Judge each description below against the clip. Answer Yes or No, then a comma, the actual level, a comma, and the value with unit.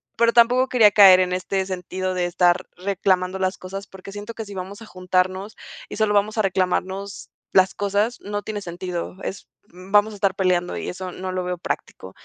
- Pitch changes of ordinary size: No, narrow, 2.0 semitones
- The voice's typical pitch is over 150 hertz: Yes, high, 190 Hz